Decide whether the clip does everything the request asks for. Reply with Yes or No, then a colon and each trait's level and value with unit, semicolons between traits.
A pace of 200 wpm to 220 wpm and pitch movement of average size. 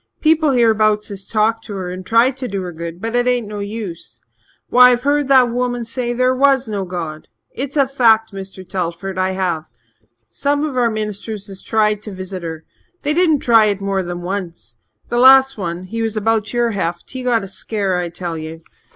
Yes: fast, 205 wpm; average, 4.8 semitones